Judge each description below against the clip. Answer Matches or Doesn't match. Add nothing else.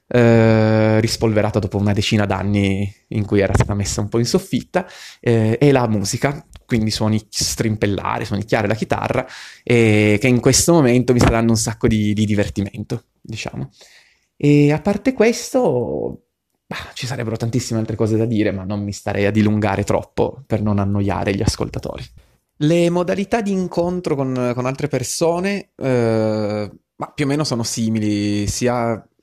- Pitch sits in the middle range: Doesn't match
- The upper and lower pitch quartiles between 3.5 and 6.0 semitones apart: Matches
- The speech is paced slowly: Doesn't match